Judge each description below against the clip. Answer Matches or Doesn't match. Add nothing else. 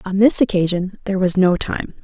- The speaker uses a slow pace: Doesn't match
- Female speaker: Matches